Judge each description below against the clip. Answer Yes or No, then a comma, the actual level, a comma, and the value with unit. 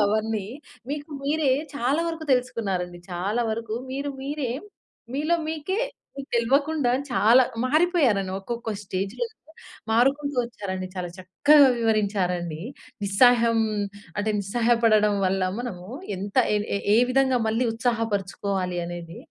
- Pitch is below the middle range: No, high, 230 Hz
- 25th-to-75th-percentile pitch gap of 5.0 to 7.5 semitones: Yes, wide, 5.6 semitones